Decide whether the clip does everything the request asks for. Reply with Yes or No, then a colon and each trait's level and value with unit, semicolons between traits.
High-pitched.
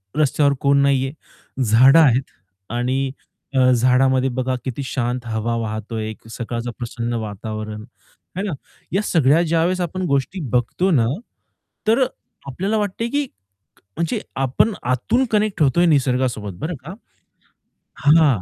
No: low, 135 Hz